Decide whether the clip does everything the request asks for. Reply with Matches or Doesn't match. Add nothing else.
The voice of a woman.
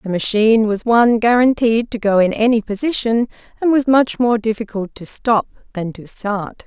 Matches